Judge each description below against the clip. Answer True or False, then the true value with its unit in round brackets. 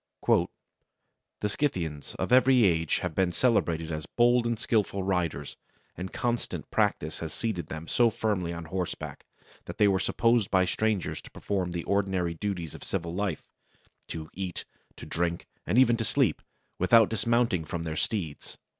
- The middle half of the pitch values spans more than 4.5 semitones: True (5.0 semitones)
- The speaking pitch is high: False (95 Hz)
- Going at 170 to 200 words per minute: False (160 wpm)